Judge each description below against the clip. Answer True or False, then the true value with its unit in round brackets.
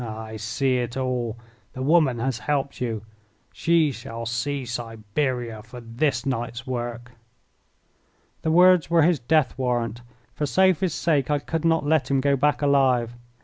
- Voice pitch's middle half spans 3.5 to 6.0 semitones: True (3.9 semitones)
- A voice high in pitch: False (130 Hz)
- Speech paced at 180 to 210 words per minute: False (155 wpm)